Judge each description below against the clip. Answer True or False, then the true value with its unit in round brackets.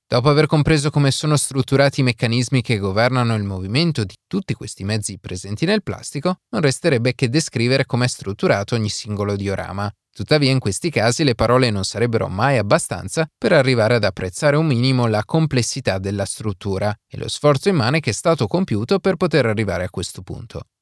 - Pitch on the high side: False (125 Hz)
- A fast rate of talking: True (180 wpm)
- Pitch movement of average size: False (5.9 semitones)